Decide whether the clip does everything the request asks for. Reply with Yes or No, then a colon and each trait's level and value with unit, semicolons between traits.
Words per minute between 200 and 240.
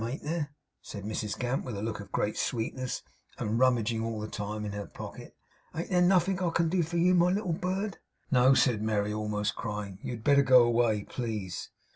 Yes: fast, 205 wpm